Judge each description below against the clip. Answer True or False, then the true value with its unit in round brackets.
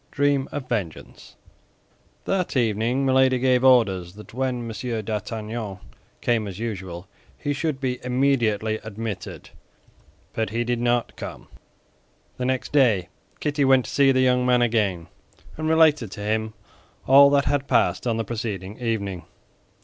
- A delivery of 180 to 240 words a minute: False (145 wpm)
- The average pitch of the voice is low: True (120 Hz)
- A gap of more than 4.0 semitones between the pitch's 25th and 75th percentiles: False (3.6 semitones)